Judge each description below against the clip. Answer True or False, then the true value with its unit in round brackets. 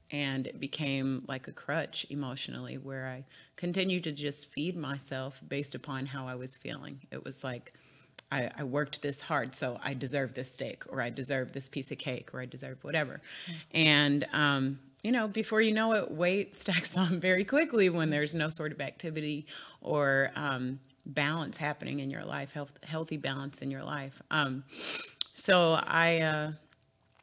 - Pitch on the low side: False (145 Hz)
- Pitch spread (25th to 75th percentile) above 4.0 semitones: False (3.0 semitones)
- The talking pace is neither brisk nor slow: True (175 wpm)